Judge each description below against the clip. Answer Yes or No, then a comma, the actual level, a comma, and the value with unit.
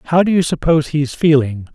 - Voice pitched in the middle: Yes, medium, 150 Hz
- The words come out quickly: Yes, fast, 240 wpm